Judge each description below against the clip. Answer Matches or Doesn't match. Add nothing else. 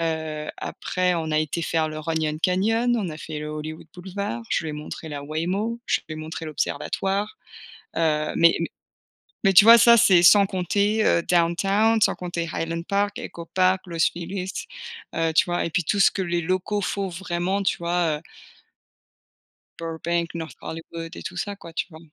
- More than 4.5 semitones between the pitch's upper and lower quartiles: Doesn't match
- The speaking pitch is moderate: Matches